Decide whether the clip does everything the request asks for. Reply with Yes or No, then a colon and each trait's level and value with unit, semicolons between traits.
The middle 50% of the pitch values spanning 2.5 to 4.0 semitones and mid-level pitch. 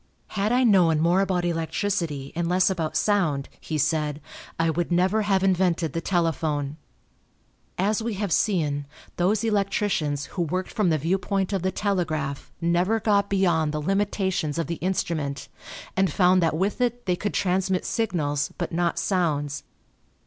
Yes: average, 3.7 semitones; medium, 180 Hz